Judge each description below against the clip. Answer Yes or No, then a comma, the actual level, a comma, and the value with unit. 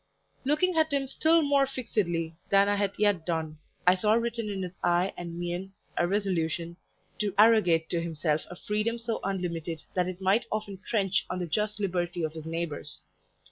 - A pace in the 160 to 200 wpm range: Yes, average, 180 wpm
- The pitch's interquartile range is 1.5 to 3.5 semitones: No, average, 3.9 semitones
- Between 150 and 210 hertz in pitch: Yes, high, 190 Hz